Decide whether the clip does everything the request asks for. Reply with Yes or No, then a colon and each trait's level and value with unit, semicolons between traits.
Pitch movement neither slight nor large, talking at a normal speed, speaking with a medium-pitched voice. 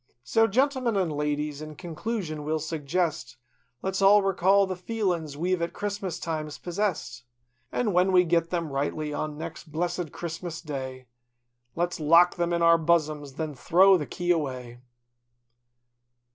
Yes: average, 3.4 semitones; average, 150 wpm; medium, 170 Hz